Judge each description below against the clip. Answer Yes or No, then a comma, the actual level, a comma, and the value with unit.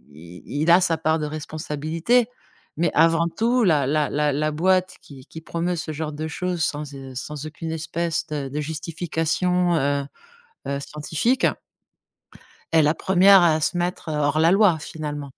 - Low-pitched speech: No, medium, 160 Hz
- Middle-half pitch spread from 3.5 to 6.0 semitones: No, narrow, 2.6 semitones